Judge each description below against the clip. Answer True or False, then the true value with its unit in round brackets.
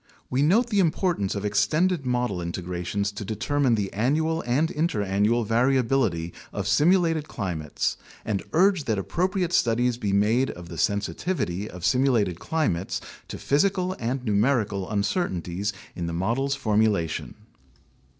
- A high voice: False (115 Hz)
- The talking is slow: True (130 wpm)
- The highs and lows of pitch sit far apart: True (7.1 semitones)